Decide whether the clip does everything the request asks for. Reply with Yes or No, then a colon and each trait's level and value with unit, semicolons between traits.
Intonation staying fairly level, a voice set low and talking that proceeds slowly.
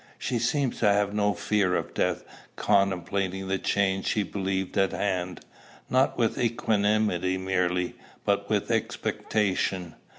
Yes: narrow, 2.0 semitones; low, 100 Hz; slow, 130 wpm